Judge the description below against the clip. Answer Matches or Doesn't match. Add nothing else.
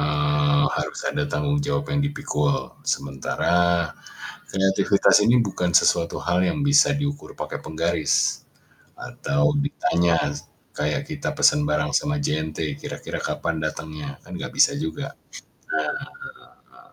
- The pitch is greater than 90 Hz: Doesn't match